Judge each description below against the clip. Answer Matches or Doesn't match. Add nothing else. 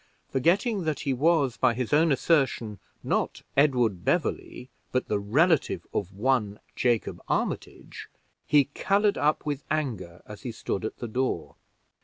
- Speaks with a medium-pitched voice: Doesn't match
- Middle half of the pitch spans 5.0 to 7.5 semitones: Matches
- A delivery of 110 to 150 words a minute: Matches